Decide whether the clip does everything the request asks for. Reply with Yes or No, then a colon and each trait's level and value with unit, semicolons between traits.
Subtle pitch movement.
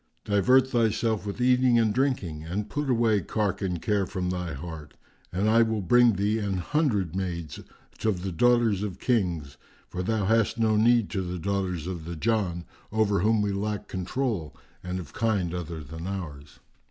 No: average, 4.1 semitones